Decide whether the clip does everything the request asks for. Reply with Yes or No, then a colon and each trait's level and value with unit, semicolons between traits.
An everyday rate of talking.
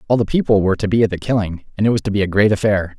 No: fast, 340 wpm